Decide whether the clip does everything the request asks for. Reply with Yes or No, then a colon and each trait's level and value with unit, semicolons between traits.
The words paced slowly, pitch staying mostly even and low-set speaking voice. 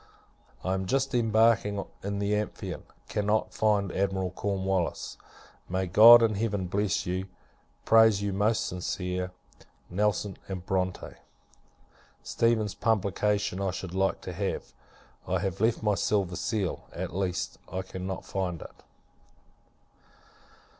Yes: slow, 125 wpm; narrow, 2.2 semitones; low, 100 Hz